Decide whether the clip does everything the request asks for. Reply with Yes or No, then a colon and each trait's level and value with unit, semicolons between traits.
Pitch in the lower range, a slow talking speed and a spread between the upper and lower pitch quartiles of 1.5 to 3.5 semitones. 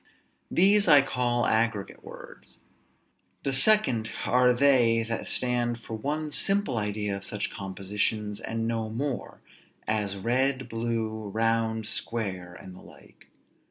Yes: low, 115 Hz; slow, 125 wpm; average, 2.9 semitones